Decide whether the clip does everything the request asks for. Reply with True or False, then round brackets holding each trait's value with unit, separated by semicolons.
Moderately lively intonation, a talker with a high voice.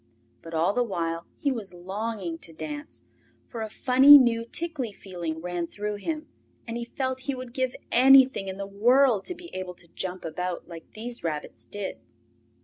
False (6.4 semitones; 215 Hz)